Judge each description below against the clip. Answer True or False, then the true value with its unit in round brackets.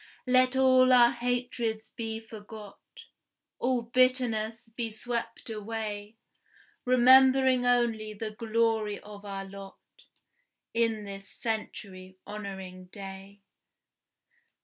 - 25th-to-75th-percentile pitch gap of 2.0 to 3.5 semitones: True (3.1 semitones)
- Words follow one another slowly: True (95 wpm)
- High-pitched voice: True (225 Hz)